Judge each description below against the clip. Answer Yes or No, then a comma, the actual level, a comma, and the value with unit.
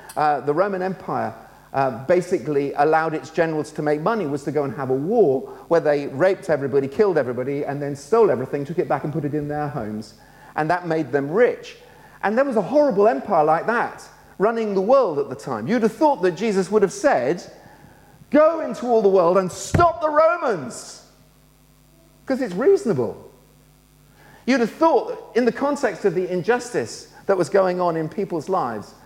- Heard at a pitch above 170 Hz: Yes, medium, 185 Hz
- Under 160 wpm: No, average, 195 wpm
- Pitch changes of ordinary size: No, wide, 7.9 semitones